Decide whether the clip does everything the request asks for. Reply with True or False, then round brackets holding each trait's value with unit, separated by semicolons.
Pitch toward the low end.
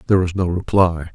True (90 Hz)